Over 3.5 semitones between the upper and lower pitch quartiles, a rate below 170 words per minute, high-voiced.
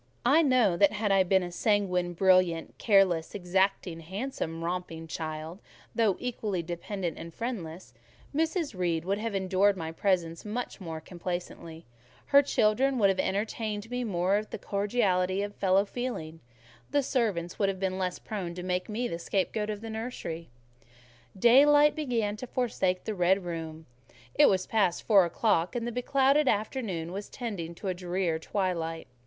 Yes: average, 4.2 semitones; average, 155 wpm; high, 195 Hz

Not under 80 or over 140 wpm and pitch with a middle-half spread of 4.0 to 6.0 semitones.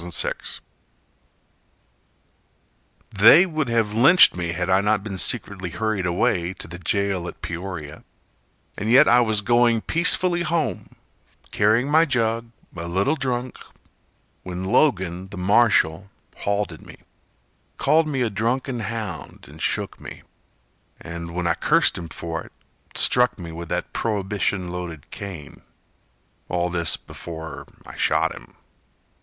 Yes: slow, 135 wpm; average, 5.3 semitones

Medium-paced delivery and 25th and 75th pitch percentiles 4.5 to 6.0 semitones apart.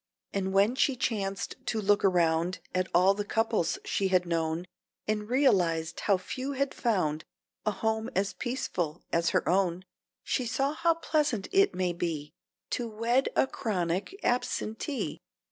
Yes: average, 150 wpm; wide, 5.6 semitones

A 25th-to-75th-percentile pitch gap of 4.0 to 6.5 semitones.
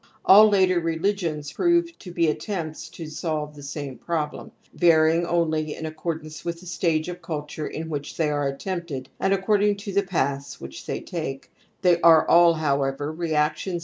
No: average, 2.9 semitones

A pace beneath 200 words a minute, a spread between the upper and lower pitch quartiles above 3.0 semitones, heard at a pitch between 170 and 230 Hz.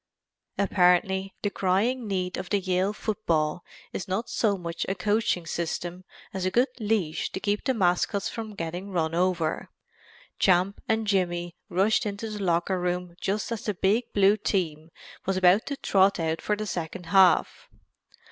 No: average, 160 wpm; average, 2.7 semitones; high, 190 Hz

